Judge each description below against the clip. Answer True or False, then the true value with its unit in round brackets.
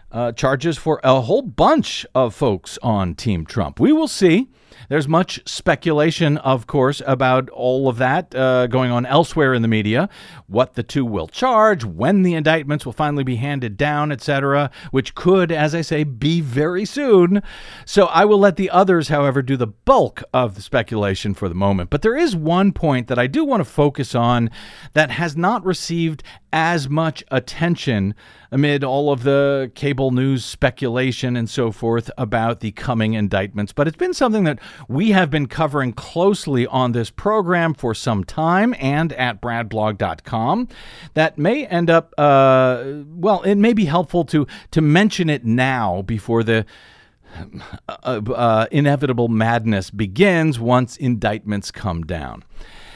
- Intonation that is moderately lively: False (5.8 semitones)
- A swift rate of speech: False (165 wpm)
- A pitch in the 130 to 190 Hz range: True (140 Hz)